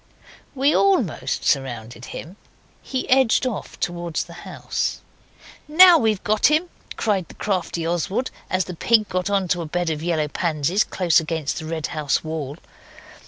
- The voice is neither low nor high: Yes, medium, 175 Hz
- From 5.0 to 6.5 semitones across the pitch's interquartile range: Yes, wide, 5.5 semitones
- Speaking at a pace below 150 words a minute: No, average, 160 wpm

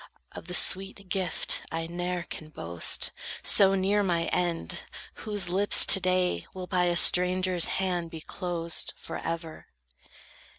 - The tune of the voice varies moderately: No, narrow, 1.9 semitones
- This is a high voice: No, medium, 180 Hz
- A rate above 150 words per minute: No, slow, 135 wpm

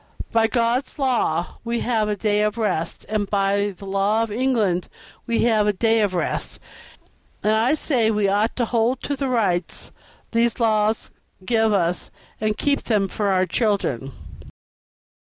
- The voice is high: Yes, high, 215 Hz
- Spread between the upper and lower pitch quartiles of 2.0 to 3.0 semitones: Yes, average, 2.7 semitones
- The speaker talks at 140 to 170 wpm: Yes, average, 160 wpm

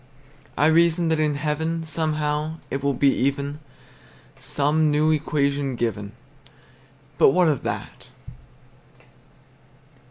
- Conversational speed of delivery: No, slow, 105 wpm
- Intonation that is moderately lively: No, narrow, 2.1 semitones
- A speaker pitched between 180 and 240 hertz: No, medium, 150 Hz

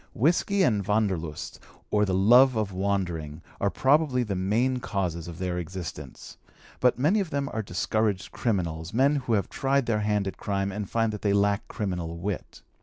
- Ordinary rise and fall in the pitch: Yes, average, 4.8 semitones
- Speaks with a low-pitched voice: Yes, low, 100 Hz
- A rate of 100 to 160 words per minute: No, average, 180 wpm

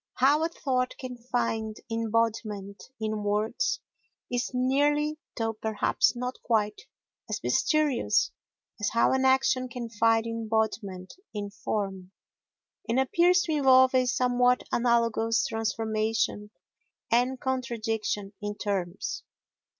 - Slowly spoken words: Yes, slow, 110 wpm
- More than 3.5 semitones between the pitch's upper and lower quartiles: No, average, 3.0 semitones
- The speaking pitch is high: Yes, high, 230 Hz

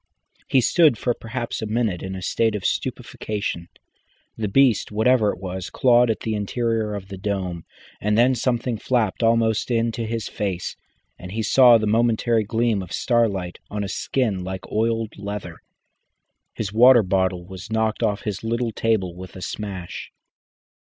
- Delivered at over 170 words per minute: No, average, 165 wpm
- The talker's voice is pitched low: Yes, low, 110 Hz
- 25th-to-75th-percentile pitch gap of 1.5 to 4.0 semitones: Yes, average, 3.3 semitones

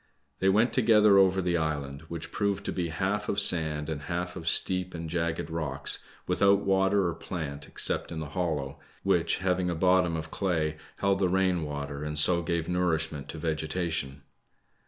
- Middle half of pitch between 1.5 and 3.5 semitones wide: Yes, average, 3.2 semitones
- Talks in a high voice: No, very low, 85 Hz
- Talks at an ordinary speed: Yes, average, 180 wpm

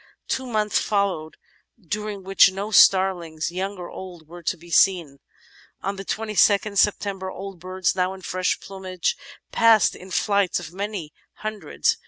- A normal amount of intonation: No, narrow, 2.2 semitones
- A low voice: No, high, 190 Hz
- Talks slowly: No, average, 155 wpm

